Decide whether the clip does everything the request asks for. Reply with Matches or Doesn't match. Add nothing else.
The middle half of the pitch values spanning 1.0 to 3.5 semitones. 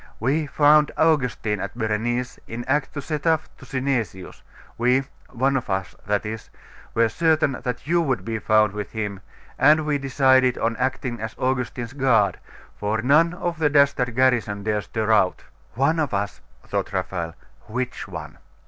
Doesn't match